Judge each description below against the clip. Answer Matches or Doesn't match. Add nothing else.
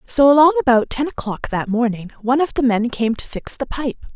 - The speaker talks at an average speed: Doesn't match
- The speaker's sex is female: Matches